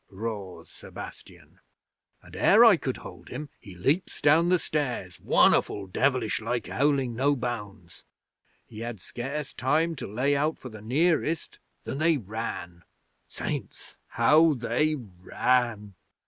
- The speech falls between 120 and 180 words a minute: Yes, slow, 135 wpm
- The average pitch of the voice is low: Yes, low, 125 Hz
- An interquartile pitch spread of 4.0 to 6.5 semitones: Yes, wide, 5.6 semitones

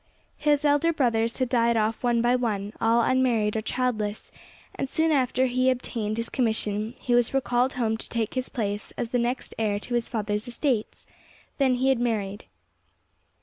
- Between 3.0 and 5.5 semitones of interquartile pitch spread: No, narrow, 2.6 semitones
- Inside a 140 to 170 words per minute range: No, average, 180 wpm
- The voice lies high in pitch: Yes, high, 240 Hz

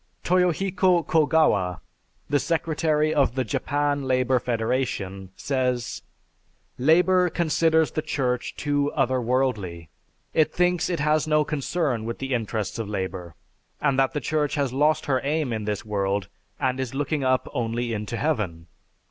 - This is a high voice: No, low, 135 Hz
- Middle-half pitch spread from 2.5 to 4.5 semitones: No, average, 5.1 semitones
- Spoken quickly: No, average, 145 wpm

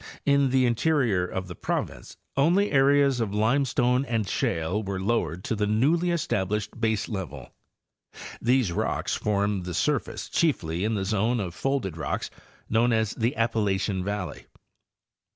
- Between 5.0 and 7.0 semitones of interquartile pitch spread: Yes, average, 5.3 semitones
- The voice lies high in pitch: No, low, 110 Hz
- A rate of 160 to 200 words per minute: No, average, 145 wpm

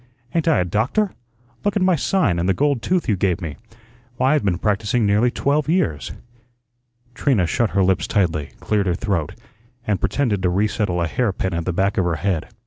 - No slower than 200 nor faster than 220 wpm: Yes, fast, 205 wpm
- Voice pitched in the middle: No, low, 100 Hz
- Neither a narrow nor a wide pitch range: No, wide, 6.5 semitones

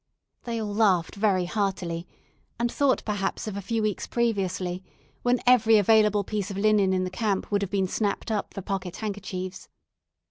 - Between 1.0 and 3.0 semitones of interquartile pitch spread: Yes, narrow, 2.6 semitones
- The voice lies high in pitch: Yes, high, 205 Hz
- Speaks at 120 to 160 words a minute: No, average, 175 wpm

